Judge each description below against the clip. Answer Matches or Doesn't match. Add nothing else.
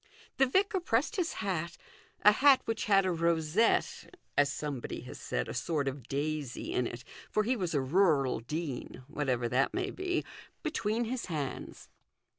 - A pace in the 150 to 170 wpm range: Matches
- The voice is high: Doesn't match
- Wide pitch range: Matches